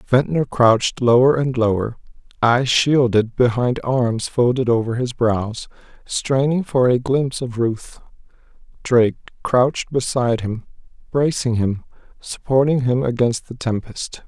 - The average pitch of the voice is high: No, low, 125 Hz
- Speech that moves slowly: Yes, slow, 125 wpm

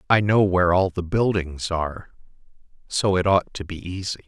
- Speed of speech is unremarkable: Yes, average, 180 wpm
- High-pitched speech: No, very low, 90 Hz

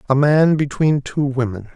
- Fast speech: No, average, 170 wpm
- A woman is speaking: No, male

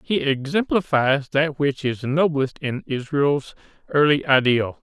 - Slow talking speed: Yes, slow, 120 wpm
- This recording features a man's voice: Yes, male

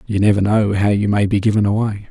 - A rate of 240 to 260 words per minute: Yes, fast, 255 wpm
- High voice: No, low, 105 Hz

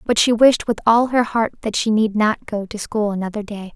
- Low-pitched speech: No, high, 215 Hz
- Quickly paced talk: Yes, fast, 255 wpm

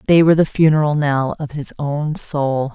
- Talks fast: No, average, 195 wpm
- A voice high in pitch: No, medium, 150 Hz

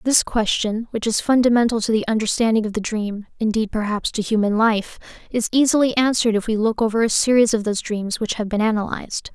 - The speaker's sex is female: Yes, female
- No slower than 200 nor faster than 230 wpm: Yes, fast, 205 wpm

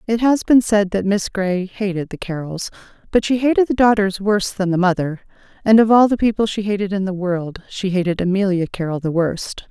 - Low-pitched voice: No, high, 195 Hz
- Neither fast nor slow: No, fast, 215 wpm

